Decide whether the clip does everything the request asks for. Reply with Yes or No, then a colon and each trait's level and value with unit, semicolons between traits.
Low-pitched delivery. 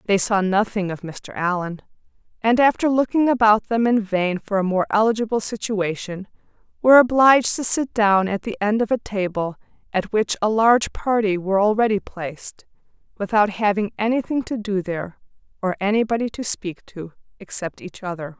No: high, 210 Hz